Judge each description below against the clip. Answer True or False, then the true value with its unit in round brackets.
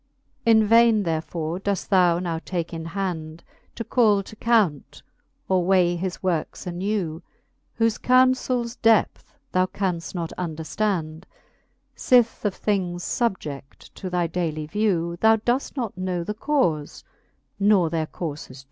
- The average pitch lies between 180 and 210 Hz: True (185 Hz)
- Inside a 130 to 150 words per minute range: True (140 wpm)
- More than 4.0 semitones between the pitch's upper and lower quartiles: True (4.4 semitones)